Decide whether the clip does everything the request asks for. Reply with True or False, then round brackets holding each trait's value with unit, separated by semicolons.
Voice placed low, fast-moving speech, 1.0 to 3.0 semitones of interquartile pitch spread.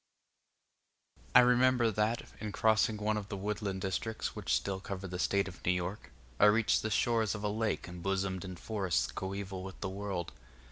False (100 Hz; 180 wpm; 2.4 semitones)